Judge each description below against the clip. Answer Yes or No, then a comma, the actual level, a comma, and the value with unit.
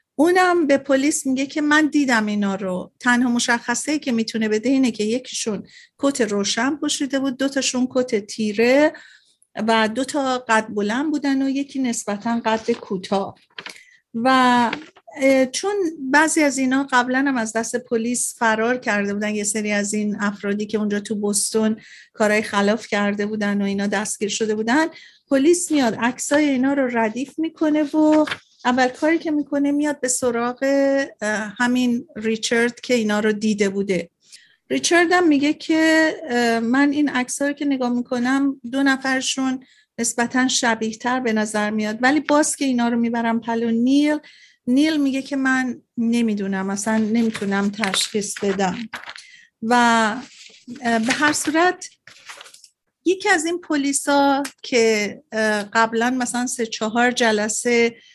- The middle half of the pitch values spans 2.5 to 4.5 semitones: Yes, average, 4.2 semitones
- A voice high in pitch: Yes, high, 245 Hz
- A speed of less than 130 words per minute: No, average, 145 wpm